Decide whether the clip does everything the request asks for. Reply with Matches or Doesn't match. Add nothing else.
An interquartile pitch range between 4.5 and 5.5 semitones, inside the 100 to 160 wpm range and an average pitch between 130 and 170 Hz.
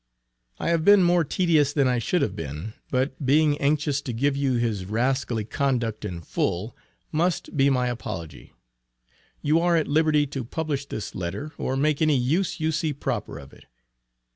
Doesn't match